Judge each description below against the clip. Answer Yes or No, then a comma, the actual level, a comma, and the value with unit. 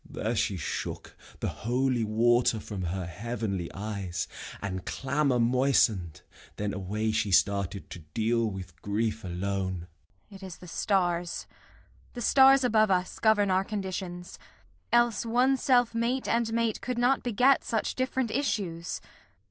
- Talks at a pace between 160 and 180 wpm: No, average, 140 wpm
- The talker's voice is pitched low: Yes, low, 130 Hz